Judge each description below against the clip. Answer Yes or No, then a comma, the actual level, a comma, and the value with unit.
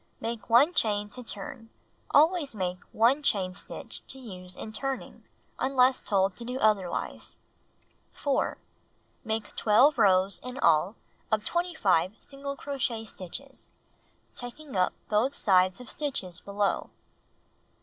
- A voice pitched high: Yes, high, 225 Hz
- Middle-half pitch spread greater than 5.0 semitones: Yes, wide, 5.5 semitones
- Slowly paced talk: Yes, slow, 125 wpm